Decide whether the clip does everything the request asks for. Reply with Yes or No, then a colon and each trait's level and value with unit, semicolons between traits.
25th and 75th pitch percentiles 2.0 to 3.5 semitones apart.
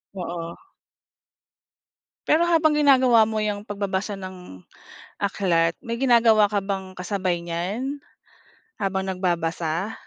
No: average, 4.4 semitones